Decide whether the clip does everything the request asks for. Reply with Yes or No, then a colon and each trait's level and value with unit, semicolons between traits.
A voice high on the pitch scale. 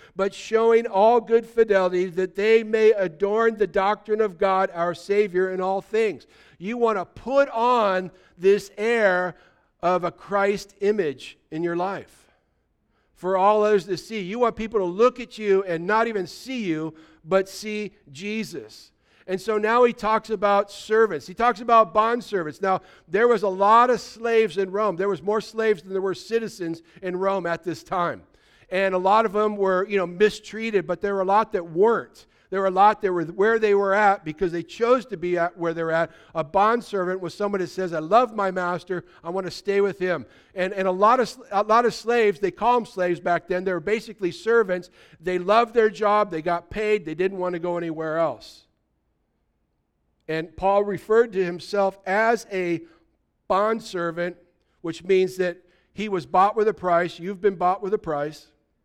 Yes: high, 195 Hz